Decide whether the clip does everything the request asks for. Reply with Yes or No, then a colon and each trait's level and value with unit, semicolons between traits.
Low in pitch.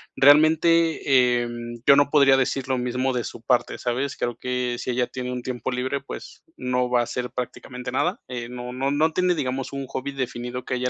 Yes: low, 125 Hz